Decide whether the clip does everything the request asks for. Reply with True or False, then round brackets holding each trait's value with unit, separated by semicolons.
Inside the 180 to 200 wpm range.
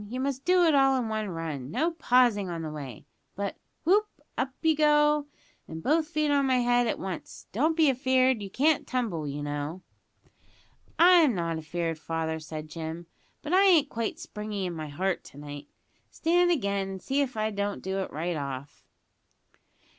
True (185 wpm)